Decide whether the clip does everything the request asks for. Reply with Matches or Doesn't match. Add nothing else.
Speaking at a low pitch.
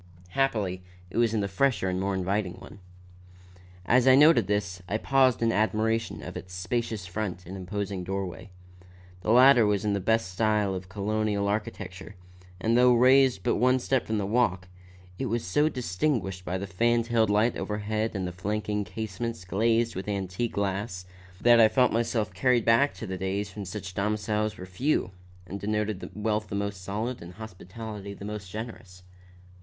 Matches